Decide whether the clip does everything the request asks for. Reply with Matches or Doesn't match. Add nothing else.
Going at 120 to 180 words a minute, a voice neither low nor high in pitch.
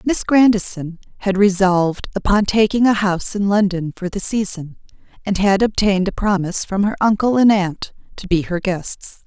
Doesn't match